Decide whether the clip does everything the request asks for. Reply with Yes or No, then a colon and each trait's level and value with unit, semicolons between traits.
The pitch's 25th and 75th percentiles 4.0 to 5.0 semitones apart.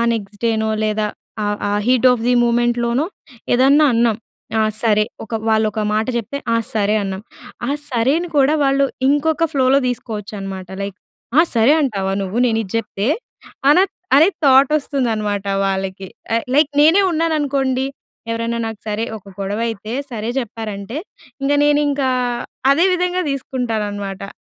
Yes: average, 4.7 semitones